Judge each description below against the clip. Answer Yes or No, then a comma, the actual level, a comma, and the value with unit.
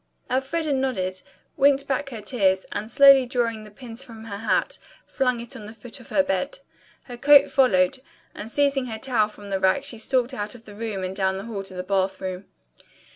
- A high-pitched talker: Yes, high, 230 Hz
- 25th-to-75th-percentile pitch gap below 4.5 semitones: No, average, 4.9 semitones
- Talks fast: Yes, fast, 210 wpm